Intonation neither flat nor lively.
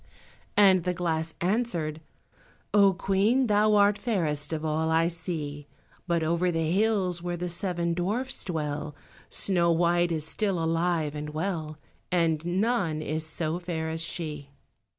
Yes: average, 3.1 semitones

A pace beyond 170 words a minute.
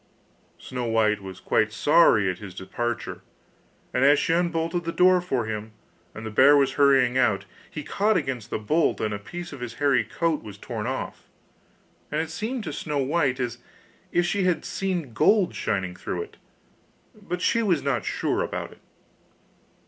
Yes: average, 180 wpm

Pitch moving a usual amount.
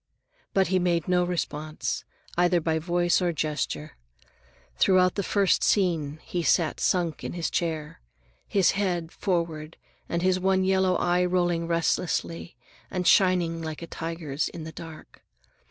No: narrow, 2.0 semitones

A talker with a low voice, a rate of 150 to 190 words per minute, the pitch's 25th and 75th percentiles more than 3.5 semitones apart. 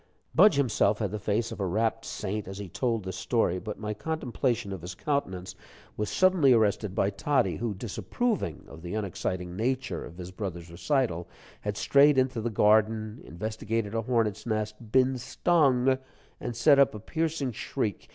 Yes: low, 110 Hz; average, 170 wpm; average, 4.6 semitones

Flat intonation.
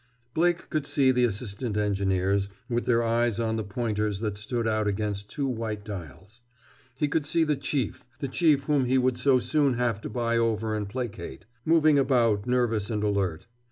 No: average, 4.0 semitones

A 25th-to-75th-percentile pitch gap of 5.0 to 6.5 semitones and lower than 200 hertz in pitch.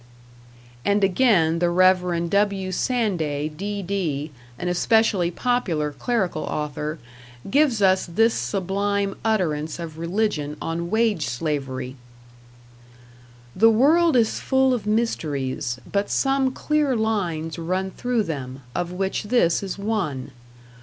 Yes: wide, 5.6 semitones; high, 190 Hz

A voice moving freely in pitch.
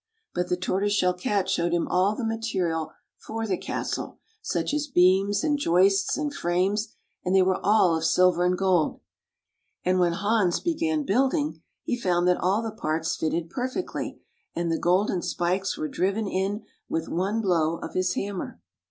No: average, 3.5 semitones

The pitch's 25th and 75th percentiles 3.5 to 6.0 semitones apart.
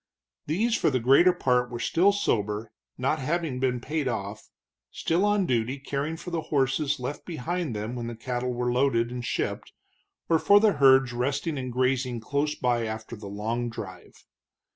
Yes: average, 4.4 semitones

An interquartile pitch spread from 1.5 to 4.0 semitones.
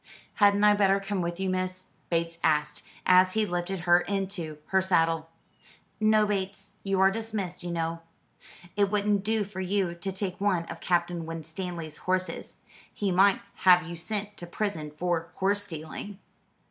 Yes: average, 2.8 semitones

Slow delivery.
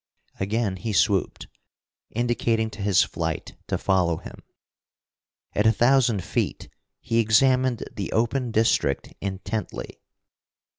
Yes: slow, 110 wpm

